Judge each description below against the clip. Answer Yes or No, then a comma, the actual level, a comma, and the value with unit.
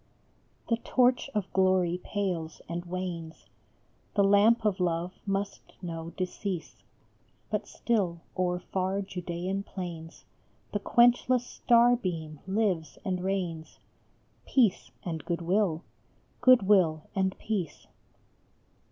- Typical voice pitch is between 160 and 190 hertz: Yes, medium, 185 Hz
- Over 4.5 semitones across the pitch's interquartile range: No, average, 3.1 semitones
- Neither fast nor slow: No, slow, 115 wpm